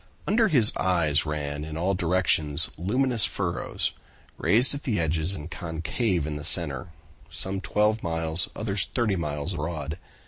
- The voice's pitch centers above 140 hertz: No, very low, 85 Hz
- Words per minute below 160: Yes, average, 145 wpm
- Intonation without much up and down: No, average, 4.7 semitones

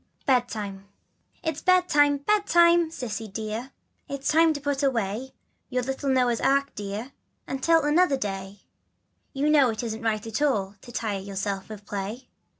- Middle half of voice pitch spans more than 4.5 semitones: Yes, average, 5.3 semitones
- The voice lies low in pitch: No, very high, 250 Hz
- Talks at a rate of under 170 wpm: Yes, average, 150 wpm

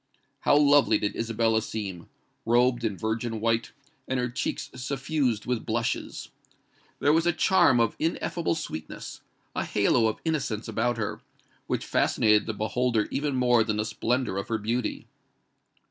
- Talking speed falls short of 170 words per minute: Yes, average, 145 wpm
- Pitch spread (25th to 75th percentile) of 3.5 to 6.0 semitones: No, average, 3.0 semitones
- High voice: No, low, 115 Hz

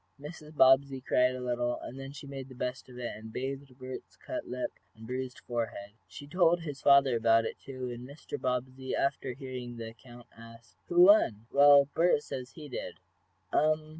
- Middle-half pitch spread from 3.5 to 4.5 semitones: No, narrow, 2.5 semitones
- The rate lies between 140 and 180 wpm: No, average, 190 wpm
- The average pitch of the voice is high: No, low, 130 Hz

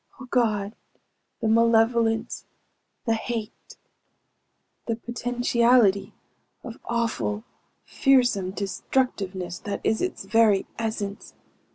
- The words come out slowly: Yes, slow, 85 wpm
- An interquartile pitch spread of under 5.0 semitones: Yes, average, 2.8 semitones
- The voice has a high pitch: Yes, high, 225 Hz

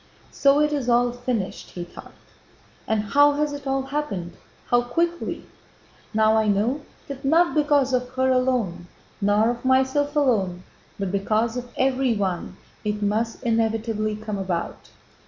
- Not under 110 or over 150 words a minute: Yes, average, 145 wpm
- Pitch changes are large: No, average, 4.3 semitones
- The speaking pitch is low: No, high, 240 Hz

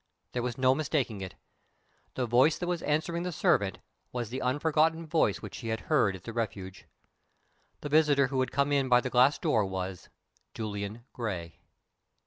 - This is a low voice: Yes, low, 125 Hz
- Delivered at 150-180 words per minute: Yes, average, 175 wpm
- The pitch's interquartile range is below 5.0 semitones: No, wide, 5.6 semitones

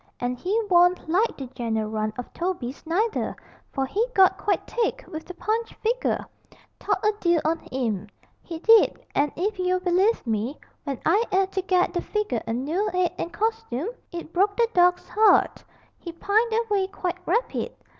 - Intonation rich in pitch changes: Yes, wide, 6.3 semitones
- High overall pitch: Yes, very high, 360 Hz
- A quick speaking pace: No, average, 175 wpm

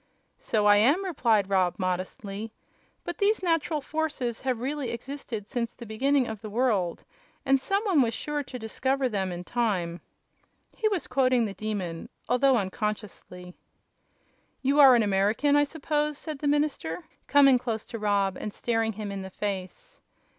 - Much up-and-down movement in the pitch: Yes, wide, 5.7 semitones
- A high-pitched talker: Yes, high, 235 Hz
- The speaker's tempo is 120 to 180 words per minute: Yes, average, 160 wpm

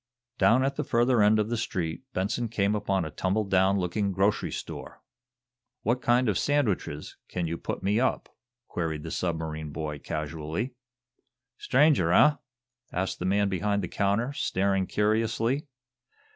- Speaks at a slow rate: No, average, 150 wpm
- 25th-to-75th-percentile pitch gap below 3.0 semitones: No, average, 4.8 semitones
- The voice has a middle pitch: No, low, 100 Hz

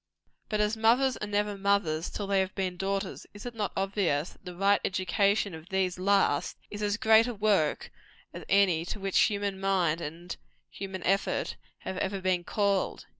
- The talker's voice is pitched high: Yes, high, 195 Hz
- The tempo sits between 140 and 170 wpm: No, average, 180 wpm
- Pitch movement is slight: Yes, narrow, 2.0 semitones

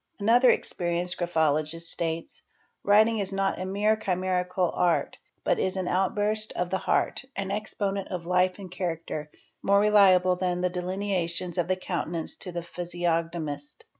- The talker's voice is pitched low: No, medium, 180 Hz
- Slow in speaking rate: No, average, 155 wpm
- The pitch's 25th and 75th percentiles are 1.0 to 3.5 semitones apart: Yes, narrow, 2.4 semitones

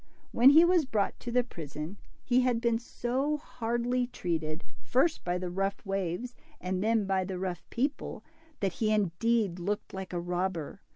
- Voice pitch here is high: Yes, high, 205 Hz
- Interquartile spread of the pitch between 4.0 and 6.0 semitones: Yes, average, 5.1 semitones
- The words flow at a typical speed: Yes, average, 170 wpm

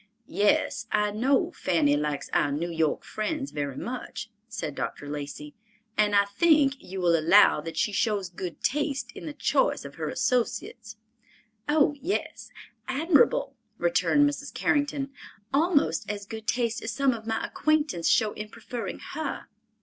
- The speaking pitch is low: No, high, 220 Hz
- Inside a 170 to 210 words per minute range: No, average, 150 wpm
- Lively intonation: Yes, wide, 8.0 semitones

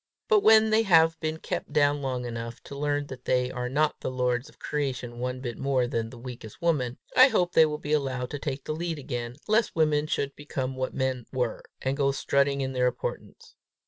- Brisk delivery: Yes, fast, 215 wpm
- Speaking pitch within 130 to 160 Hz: Yes, low, 135 Hz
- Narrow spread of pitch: No, average, 3.3 semitones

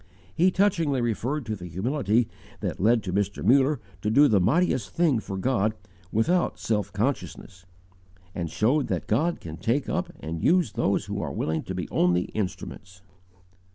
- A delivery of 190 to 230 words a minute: No, average, 165 wpm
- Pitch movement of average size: No, wide, 7.2 semitones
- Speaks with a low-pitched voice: Yes, low, 115 Hz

